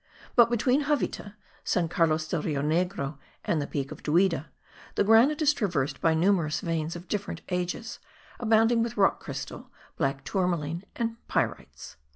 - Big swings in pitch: Yes, wide, 6.2 semitones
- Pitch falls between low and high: Yes, medium, 180 Hz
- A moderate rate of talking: Yes, average, 155 wpm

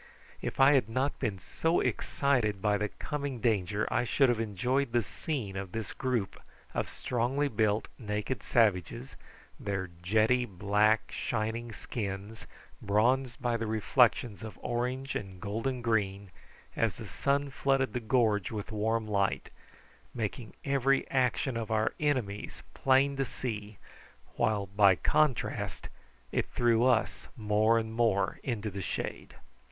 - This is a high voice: No, low, 115 Hz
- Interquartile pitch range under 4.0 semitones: Yes, average, 3.6 semitones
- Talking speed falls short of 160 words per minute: Yes, average, 140 wpm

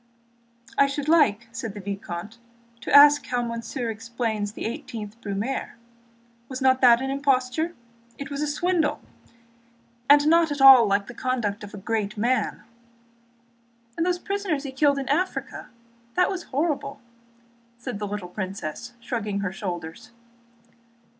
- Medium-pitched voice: No, high, 245 Hz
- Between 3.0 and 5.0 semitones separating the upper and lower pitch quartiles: No, wide, 5.4 semitones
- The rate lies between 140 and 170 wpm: Yes, average, 145 wpm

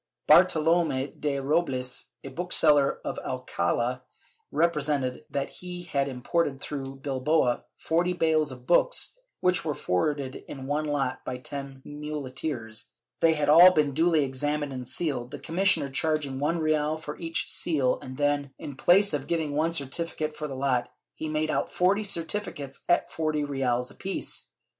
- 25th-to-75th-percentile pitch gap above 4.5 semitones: No, average, 3.2 semitones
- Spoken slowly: No, average, 150 wpm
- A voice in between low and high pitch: Yes, medium, 145 Hz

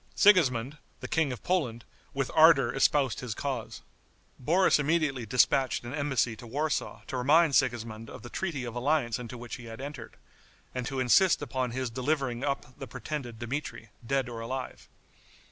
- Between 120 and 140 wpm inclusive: No, average, 165 wpm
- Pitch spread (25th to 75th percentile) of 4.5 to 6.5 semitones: No, average, 3.5 semitones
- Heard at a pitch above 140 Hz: No, low, 130 Hz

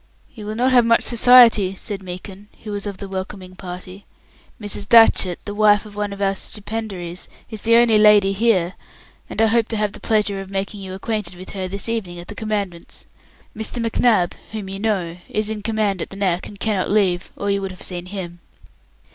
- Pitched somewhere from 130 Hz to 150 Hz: No, high, 205 Hz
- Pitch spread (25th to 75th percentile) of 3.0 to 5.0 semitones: No, narrow, 2.5 semitones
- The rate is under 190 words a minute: No, fast, 205 wpm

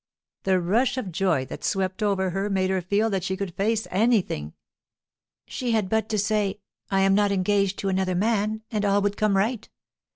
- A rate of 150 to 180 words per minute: No, average, 195 wpm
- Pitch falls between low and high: No, high, 200 Hz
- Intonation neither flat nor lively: No, narrow, 2.2 semitones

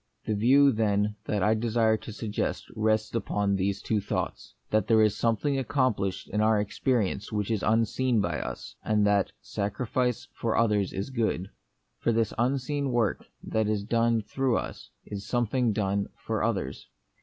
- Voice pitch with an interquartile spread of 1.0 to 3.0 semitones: Yes, narrow, 2.5 semitones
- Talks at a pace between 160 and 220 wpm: Yes, average, 165 wpm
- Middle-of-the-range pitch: No, low, 110 Hz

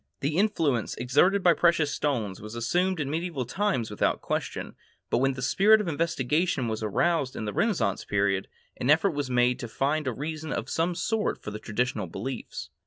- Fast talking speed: No, average, 185 wpm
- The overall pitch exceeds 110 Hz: Yes, medium, 140 Hz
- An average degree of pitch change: No, wide, 6.4 semitones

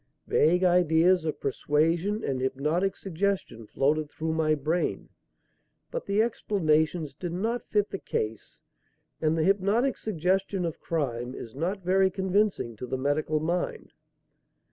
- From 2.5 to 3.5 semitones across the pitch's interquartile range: No, average, 4.2 semitones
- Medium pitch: Yes, medium, 165 Hz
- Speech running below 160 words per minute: Yes, slow, 135 wpm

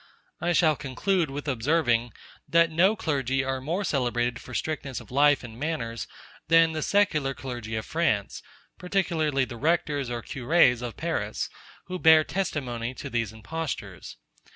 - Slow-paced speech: No, average, 150 wpm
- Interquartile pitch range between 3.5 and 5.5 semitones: Yes, average, 5.1 semitones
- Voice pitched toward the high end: No, medium, 140 Hz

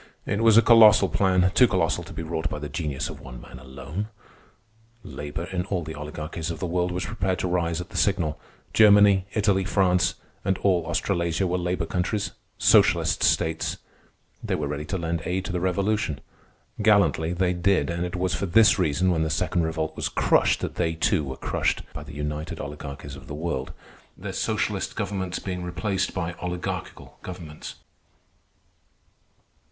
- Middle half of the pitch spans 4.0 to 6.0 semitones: No, average, 3.2 semitones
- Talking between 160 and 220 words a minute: Yes, average, 170 wpm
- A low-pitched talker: Yes, very low, 90 Hz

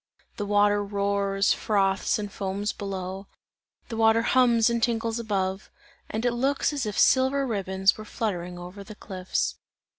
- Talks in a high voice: Yes, high, 205 Hz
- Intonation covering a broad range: No, average, 2.9 semitones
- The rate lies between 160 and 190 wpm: No, average, 150 wpm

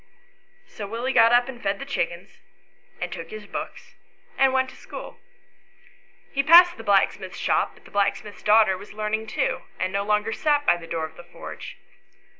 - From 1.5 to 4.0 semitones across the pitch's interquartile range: No, average, 4.8 semitones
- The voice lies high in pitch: Yes, high, 220 Hz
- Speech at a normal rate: Yes, average, 185 wpm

